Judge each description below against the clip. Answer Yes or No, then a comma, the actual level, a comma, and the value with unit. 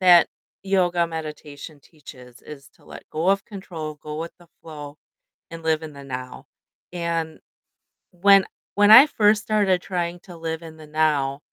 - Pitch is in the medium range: Yes, medium, 165 Hz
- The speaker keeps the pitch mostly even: No, average, 3.1 semitones